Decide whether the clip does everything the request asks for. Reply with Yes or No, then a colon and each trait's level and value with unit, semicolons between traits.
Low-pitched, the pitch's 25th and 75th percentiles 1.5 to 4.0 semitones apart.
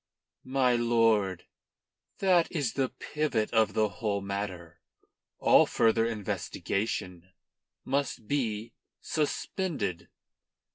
No: low, 115 Hz; average, 4.6 semitones